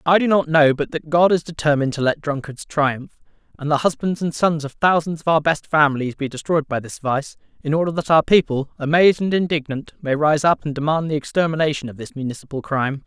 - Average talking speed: No, fast, 220 wpm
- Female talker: No, male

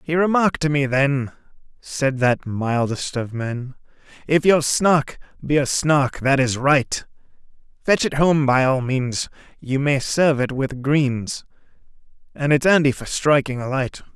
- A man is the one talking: Yes, male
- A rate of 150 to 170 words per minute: Yes, average, 155 wpm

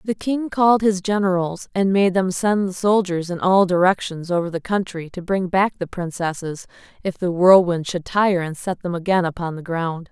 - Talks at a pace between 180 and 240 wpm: Yes, average, 200 wpm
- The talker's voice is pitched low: No, medium, 185 Hz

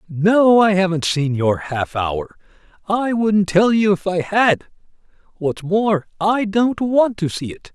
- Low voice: No, high, 190 Hz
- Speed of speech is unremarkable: Yes, average, 185 wpm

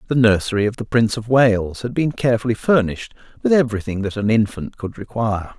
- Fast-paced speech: No, average, 195 wpm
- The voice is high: No, low, 115 Hz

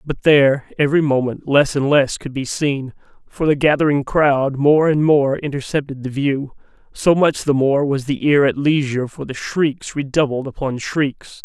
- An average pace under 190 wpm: Yes, average, 180 wpm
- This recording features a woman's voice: No, male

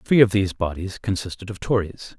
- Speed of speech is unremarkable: Yes, average, 190 wpm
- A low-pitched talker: Yes, low, 100 Hz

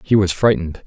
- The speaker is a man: Yes, male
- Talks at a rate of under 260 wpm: Yes, fast, 210 wpm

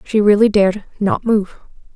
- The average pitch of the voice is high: Yes, high, 205 Hz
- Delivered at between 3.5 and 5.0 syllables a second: Yes, 4.9 syllables/s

